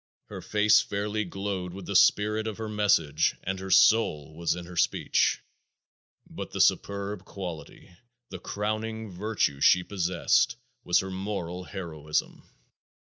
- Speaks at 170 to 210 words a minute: No, slow, 135 wpm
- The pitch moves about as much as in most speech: Yes, average, 3.2 semitones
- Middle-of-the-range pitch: No, very low, 95 Hz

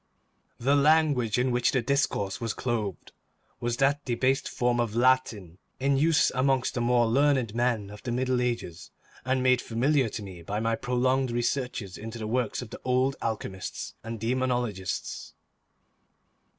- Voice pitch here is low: Yes, low, 120 Hz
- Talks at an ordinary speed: Yes, average, 155 wpm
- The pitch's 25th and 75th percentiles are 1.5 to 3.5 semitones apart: Yes, narrow, 2.5 semitones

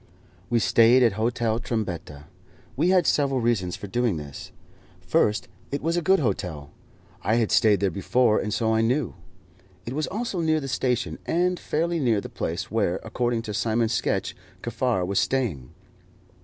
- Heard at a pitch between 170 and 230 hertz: No, low, 115 Hz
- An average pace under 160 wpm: No, average, 170 wpm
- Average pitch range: Yes, average, 4.6 semitones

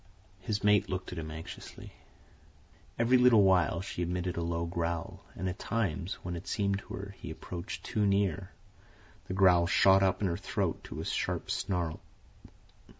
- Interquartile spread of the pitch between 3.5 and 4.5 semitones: No, narrow, 2.6 semitones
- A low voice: Yes, very low, 95 Hz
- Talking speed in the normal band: Yes, average, 170 wpm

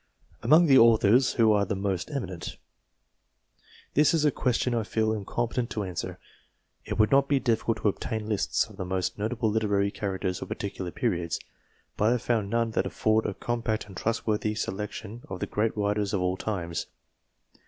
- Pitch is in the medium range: No, low, 110 Hz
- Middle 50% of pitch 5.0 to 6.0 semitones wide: No, average, 2.8 semitones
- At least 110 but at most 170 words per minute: No, average, 185 wpm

